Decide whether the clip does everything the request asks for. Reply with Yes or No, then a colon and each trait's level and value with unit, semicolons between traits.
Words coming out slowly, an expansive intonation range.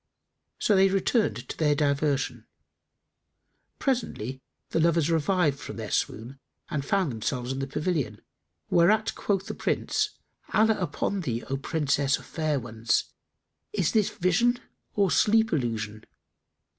Yes: slow, 130 wpm; wide, 6.6 semitones